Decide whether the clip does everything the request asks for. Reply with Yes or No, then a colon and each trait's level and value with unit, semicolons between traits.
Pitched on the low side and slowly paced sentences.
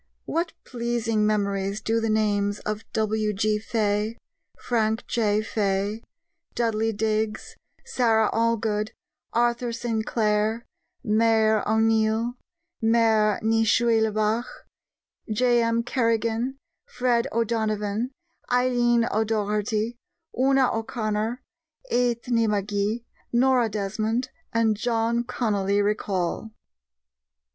No: high, 220 Hz; slow, 85 wpm